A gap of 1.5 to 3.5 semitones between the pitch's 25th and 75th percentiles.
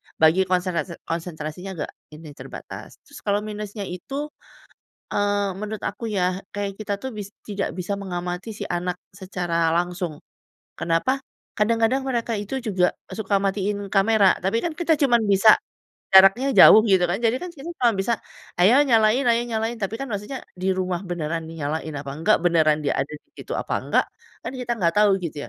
No: average, 4.1 semitones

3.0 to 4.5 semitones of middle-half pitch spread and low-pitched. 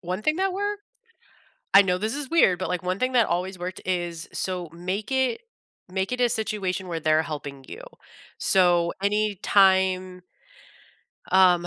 No: average, 3.5 semitones; medium, 185 Hz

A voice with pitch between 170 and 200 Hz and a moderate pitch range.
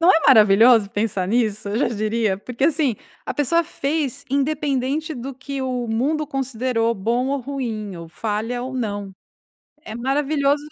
No: very high, 250 Hz; average, 4.3 semitones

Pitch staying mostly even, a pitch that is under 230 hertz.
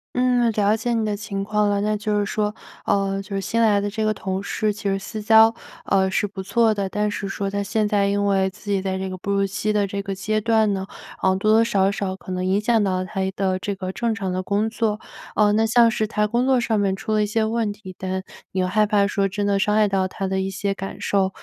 Yes: narrow, 1.8 semitones; high, 205 Hz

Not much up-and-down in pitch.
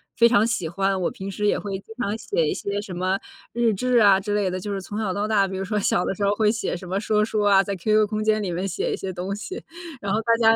Yes: narrow, 2.0 semitones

